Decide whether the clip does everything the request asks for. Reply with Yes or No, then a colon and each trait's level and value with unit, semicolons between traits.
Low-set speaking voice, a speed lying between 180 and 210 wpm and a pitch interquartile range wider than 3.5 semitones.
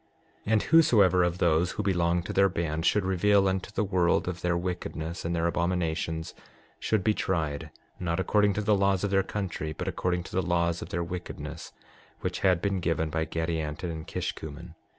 No: very low, 90 Hz; average, 190 wpm; average, 2.8 semitones